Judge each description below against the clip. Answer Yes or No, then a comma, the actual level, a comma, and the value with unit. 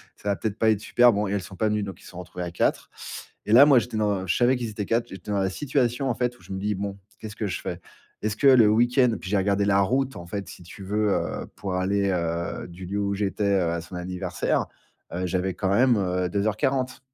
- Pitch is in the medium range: No, low, 100 Hz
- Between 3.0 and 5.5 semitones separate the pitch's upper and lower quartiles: Yes, average, 3.3 semitones